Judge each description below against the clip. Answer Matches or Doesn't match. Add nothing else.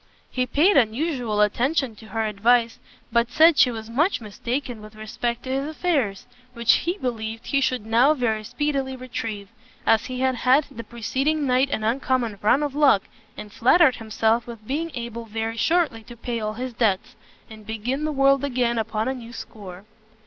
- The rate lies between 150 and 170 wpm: Doesn't match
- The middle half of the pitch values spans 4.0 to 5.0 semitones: Doesn't match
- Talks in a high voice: Matches